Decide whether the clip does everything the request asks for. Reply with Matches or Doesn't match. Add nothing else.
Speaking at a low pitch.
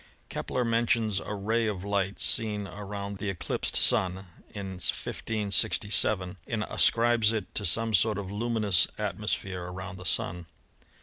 Matches